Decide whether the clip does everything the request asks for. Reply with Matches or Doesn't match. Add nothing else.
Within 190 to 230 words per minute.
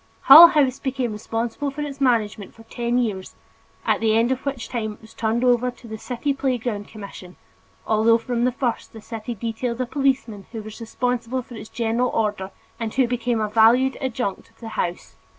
Matches